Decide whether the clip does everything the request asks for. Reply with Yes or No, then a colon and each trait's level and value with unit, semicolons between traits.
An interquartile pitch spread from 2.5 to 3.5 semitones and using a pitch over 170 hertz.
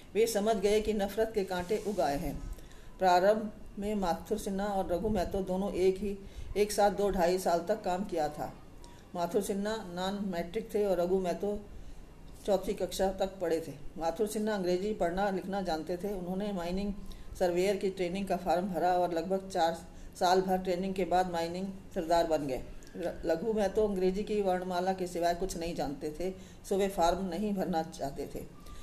Yes: average, 2.8 semitones; high, 190 Hz